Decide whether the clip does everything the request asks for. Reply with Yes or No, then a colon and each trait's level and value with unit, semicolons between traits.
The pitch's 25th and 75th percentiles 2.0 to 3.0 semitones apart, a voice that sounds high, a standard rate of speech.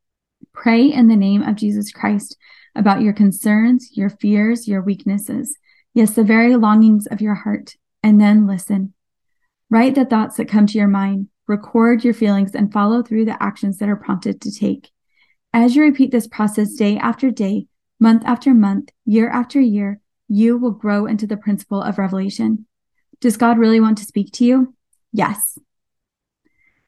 Yes: narrow, 2.4 semitones; high, 220 Hz; average, 170 wpm